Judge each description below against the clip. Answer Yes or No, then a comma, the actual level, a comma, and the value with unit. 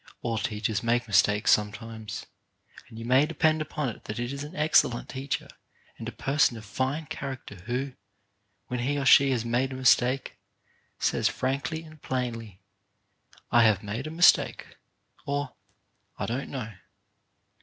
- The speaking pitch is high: No, low, 125 Hz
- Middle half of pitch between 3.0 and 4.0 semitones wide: Yes, average, 3.6 semitones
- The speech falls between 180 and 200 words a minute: No, average, 155 wpm